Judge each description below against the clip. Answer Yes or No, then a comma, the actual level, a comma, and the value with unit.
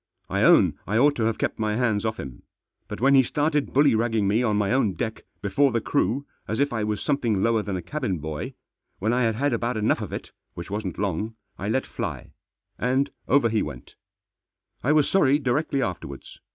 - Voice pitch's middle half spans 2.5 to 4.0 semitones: No, average, 4.4 semitones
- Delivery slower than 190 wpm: No, fast, 205 wpm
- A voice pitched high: No, low, 115 Hz